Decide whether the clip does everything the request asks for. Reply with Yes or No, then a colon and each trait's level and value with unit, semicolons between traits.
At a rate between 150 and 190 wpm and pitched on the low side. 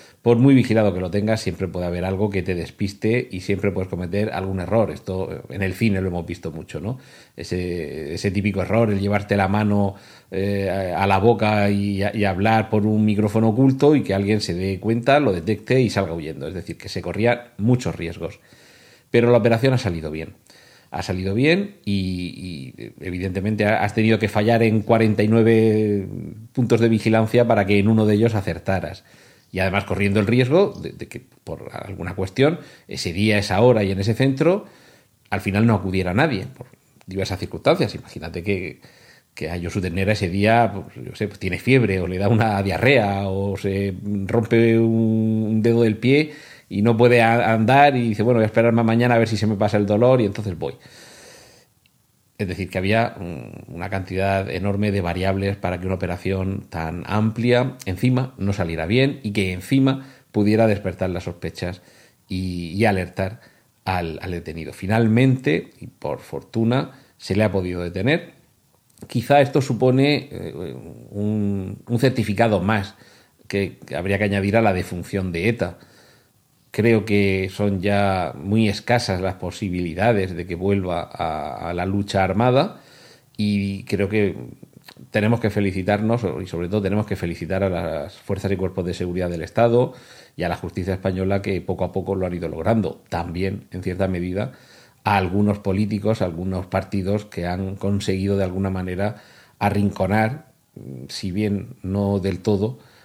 Yes: average, 170 wpm; low, 100 Hz